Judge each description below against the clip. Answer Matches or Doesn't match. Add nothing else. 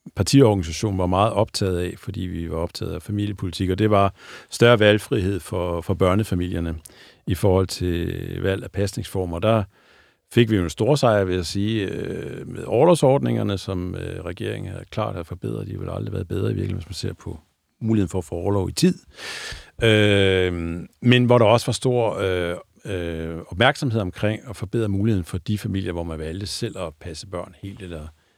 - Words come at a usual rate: Matches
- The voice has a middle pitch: Doesn't match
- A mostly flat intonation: Doesn't match